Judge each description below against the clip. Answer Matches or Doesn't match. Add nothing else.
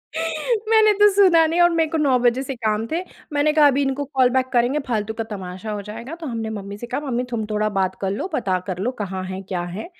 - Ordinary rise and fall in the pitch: Doesn't match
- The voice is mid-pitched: Doesn't match